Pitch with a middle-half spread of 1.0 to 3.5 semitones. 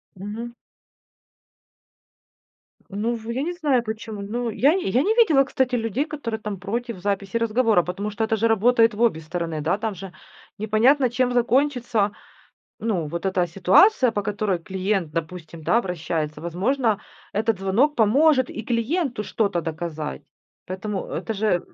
No: average, 4.3 semitones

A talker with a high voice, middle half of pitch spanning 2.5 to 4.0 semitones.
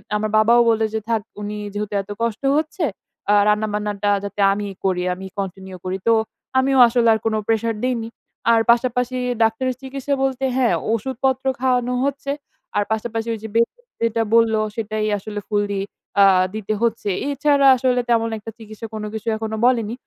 Yes: high, 225 Hz; average, 3.0 semitones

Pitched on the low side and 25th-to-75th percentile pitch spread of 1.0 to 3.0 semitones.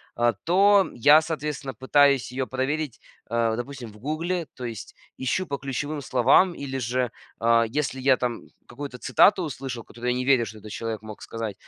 No: low, 130 Hz; average, 3.8 semitones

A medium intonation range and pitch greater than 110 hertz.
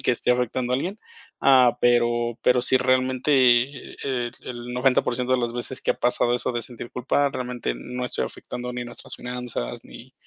No: narrow, 1.0 semitones; low, 125 Hz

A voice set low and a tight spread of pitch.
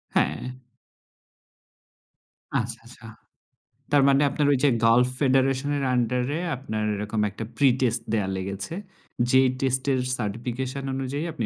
No: low, 130 Hz; average, 3.1 semitones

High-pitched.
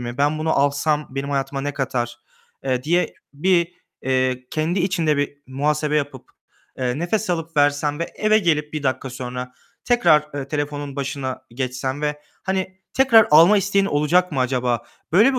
No: medium, 145 Hz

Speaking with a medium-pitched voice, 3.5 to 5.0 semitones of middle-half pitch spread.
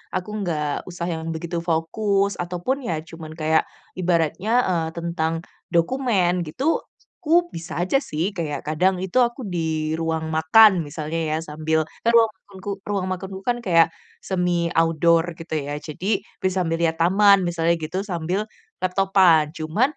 No: medium, 170 Hz; average, 3.0 semitones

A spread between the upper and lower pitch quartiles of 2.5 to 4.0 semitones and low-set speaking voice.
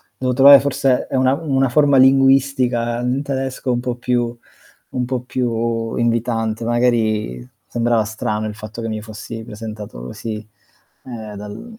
Yes: average, 2.8 semitones; low, 120 Hz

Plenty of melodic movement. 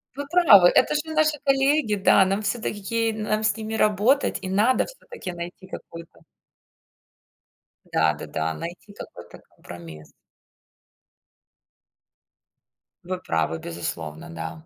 Yes: wide, 6.1 semitones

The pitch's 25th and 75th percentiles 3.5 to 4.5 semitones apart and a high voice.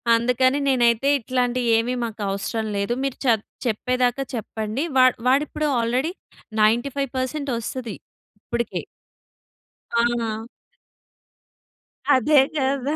No: narrow, 2.5 semitones; high, 245 Hz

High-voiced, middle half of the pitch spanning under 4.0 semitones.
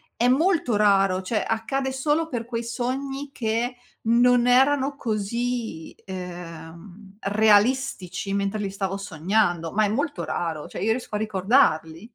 No: high, 220 Hz; average, 4.3 semitones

